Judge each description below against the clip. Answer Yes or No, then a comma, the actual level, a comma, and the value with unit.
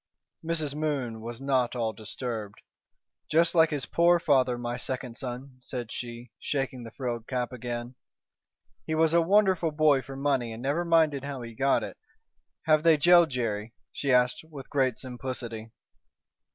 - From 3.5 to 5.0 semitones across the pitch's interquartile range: Yes, average, 4.2 semitones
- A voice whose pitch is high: No, low, 130 Hz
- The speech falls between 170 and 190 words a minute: No, average, 160 wpm